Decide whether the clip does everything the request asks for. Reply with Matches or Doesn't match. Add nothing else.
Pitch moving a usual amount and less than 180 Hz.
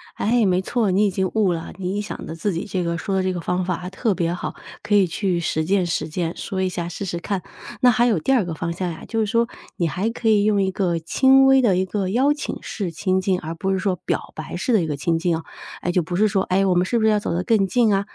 Doesn't match